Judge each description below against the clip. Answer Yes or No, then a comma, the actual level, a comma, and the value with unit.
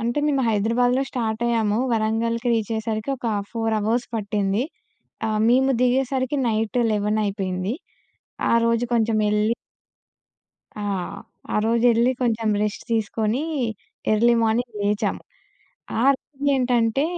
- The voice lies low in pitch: No, high, 225 Hz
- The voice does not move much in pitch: Yes, narrow, 2.2 semitones